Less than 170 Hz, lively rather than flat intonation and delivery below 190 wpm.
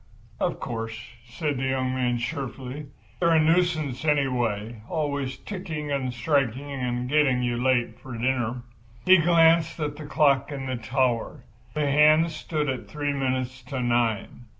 No: low, 135 Hz; average, 3.6 semitones; average, 150 wpm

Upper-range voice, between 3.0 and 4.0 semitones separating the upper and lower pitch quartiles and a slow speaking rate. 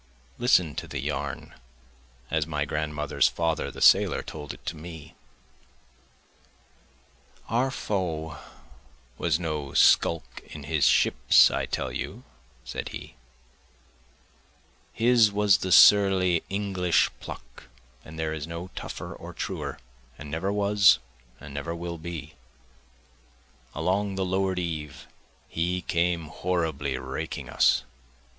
No: very low, 85 Hz; average, 3.7 semitones; slow, 120 wpm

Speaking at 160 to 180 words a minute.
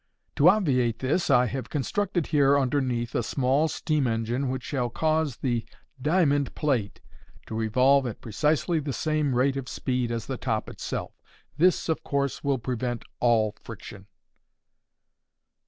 No: average, 145 wpm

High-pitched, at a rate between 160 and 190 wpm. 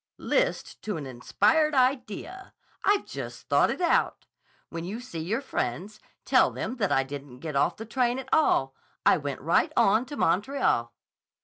Yes: high, 210 Hz; average, 170 wpm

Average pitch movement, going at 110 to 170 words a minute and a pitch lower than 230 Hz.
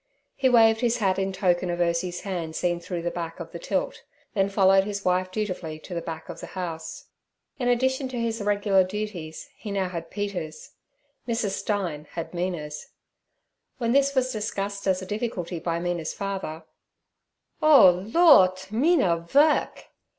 Yes: average, 4.2 semitones; average, 160 wpm; high, 190 Hz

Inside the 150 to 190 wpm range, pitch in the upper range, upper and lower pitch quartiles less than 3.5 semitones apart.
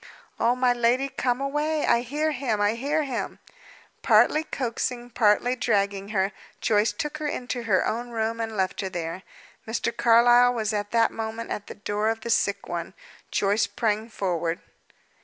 Yes: average, 170 wpm; high, 230 Hz; average, 3.0 semitones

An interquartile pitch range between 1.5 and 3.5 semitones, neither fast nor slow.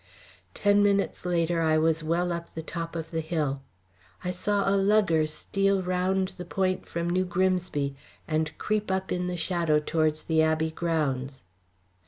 Yes: average, 2.9 semitones; average, 165 wpm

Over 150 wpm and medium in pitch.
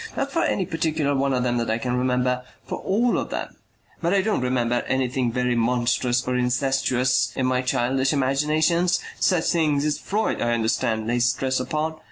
No: average, 185 wpm; low, 130 Hz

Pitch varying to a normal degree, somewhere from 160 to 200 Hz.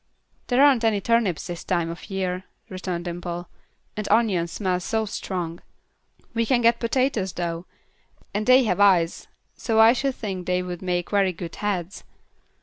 Yes: average, 4.1 semitones; high, 190 Hz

